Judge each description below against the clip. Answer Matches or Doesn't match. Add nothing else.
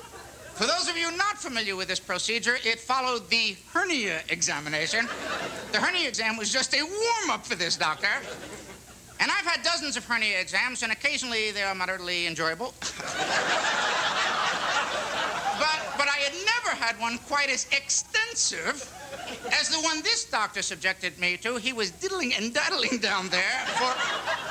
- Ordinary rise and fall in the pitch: Doesn't match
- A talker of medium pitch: Doesn't match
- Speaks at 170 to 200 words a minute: Doesn't match